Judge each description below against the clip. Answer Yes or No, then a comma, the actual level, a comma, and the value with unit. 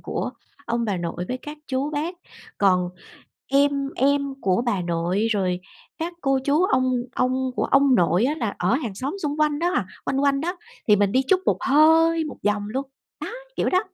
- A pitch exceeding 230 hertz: Yes, very high, 265 Hz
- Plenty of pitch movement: Yes, wide, 6.2 semitones